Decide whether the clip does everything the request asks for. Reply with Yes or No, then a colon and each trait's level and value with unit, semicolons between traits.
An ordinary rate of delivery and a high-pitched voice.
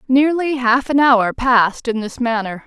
Yes: average, 180 wpm; high, 245 Hz